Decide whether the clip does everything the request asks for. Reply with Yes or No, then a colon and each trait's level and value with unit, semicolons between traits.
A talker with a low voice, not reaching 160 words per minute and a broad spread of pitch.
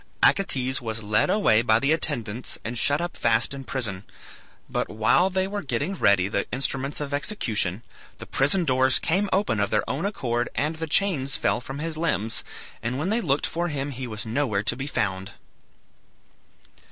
No: low, 130 Hz; average, 180 wpm; wide, 6.0 semitones